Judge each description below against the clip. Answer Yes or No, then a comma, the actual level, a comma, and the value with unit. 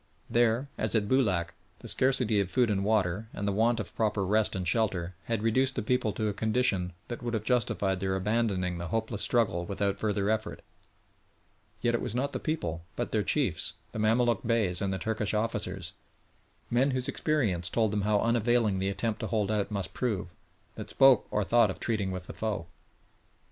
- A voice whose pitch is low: Yes, low, 110 Hz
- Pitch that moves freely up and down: No, average, 3.2 semitones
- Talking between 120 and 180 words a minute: No, average, 195 wpm